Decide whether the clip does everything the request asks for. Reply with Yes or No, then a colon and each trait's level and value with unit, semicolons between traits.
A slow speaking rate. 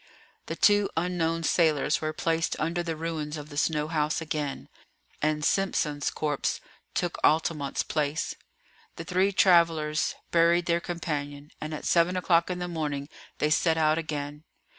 No: average, 150 wpm